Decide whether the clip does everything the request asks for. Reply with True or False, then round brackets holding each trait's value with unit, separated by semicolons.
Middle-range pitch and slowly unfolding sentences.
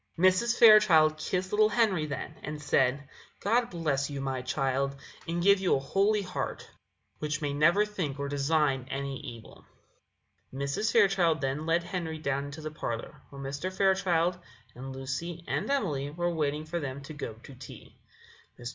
False (155 Hz; 165 wpm)